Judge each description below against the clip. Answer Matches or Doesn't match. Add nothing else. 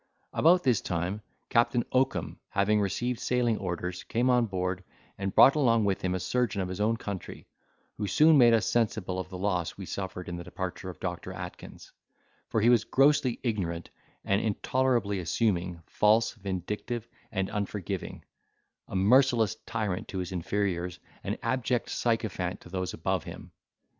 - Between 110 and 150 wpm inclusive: Doesn't match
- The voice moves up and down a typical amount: Matches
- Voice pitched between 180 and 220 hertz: Doesn't match